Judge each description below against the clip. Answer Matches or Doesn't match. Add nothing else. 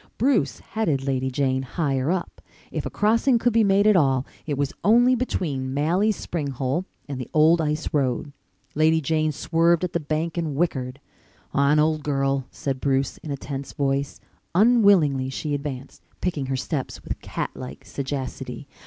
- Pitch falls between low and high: Matches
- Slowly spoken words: Doesn't match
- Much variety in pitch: Doesn't match